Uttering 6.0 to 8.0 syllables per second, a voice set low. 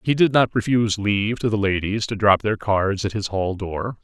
No: 5.1 syllables/s; low, 105 Hz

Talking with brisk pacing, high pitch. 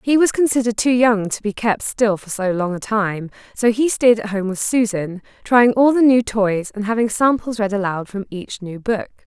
Yes: fast, 225 wpm; high, 215 Hz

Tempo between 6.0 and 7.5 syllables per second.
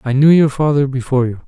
Yes: 6.8 syllables/s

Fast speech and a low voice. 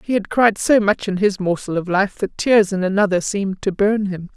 No: fast, 250 wpm; high, 200 Hz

